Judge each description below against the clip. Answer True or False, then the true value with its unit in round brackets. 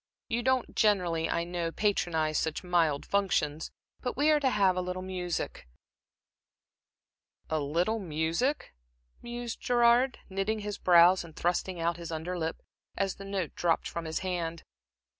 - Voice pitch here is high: False (180 Hz)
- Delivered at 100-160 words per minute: True (150 wpm)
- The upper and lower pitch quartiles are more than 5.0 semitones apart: False (4.0 semitones)